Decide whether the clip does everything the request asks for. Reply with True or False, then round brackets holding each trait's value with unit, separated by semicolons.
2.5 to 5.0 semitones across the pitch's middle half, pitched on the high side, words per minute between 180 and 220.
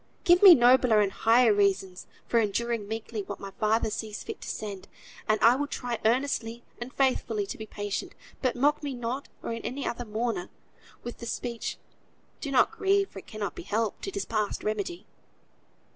True (3.4 semitones; 230 Hz; 185 wpm)